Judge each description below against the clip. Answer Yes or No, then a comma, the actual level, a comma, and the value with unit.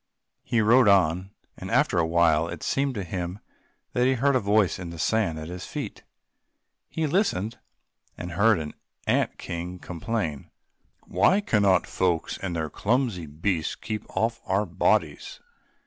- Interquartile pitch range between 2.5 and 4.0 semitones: No, average, 4.9 semitones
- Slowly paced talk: No, average, 155 wpm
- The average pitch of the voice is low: Yes, very low, 95 Hz